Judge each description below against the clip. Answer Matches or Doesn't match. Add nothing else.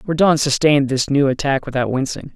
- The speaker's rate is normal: Matches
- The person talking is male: Matches